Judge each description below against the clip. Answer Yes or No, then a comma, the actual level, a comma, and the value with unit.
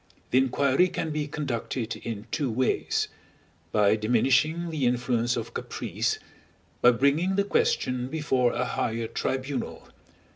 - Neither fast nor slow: No, slow, 125 wpm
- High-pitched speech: No, low, 130 Hz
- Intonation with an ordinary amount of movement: Yes, average, 4.0 semitones